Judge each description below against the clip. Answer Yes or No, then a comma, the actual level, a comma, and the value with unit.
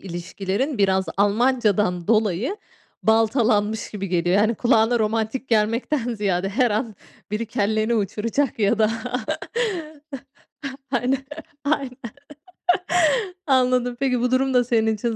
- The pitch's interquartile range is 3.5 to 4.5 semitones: No, average, 3.1 semitones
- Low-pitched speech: No, high, 220 Hz